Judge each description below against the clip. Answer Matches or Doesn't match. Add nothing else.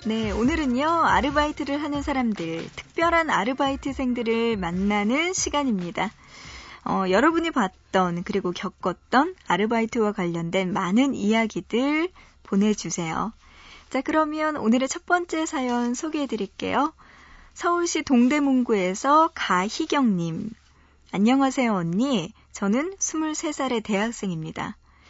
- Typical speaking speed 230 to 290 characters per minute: Matches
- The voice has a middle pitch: Doesn't match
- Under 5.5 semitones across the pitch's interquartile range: Doesn't match